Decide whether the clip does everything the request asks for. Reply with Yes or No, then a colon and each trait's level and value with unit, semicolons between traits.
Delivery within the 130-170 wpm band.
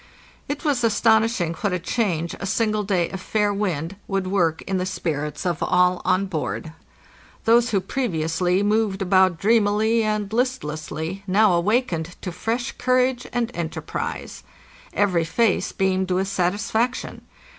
Yes: average, 140 wpm